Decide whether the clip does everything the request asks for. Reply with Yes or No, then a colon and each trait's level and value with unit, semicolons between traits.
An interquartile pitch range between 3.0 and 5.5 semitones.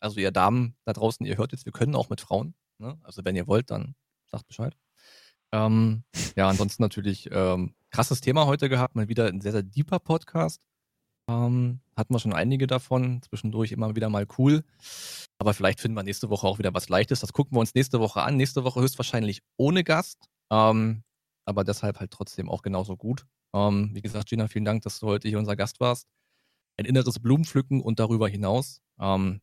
Yes: average, 4.0 semitones